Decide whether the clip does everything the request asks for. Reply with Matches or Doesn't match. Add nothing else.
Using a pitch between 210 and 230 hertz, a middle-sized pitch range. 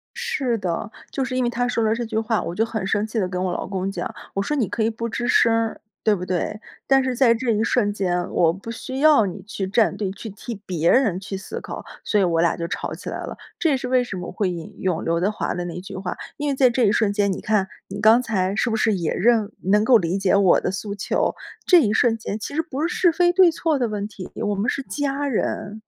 Matches